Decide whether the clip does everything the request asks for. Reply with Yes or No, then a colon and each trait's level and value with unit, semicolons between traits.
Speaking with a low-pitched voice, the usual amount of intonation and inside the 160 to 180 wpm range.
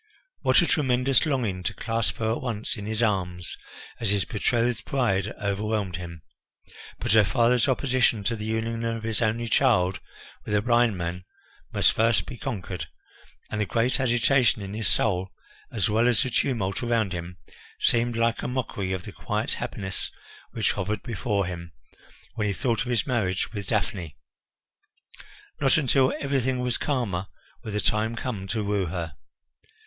Yes: low, 110 Hz; average, 3.8 semitones; average, 165 wpm